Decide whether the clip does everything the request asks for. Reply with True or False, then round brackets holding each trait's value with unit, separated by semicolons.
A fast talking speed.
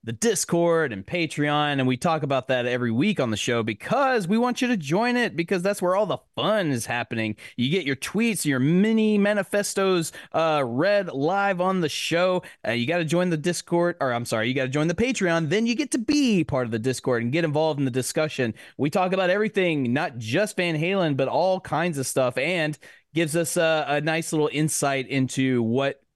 True (220 wpm)